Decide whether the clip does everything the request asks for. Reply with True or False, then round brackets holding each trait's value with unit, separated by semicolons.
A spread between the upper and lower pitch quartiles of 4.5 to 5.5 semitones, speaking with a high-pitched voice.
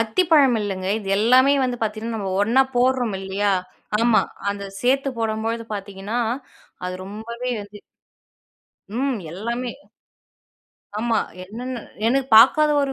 False (3.5 semitones; 230 Hz)